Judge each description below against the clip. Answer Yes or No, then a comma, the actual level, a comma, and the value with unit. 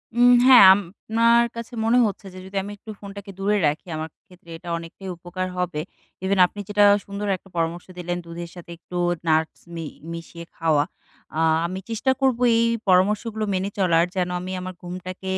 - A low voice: No, medium, 185 Hz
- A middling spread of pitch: Yes, average, 3.2 semitones